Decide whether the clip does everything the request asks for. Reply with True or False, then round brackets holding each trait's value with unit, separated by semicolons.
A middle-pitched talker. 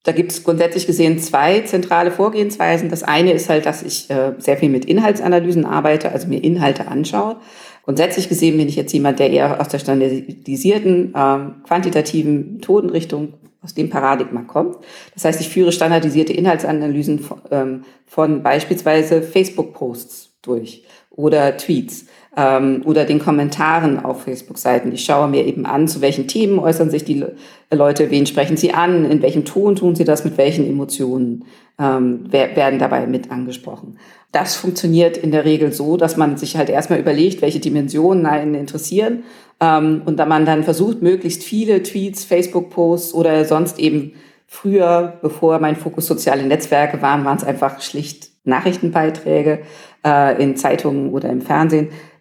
True (155 Hz)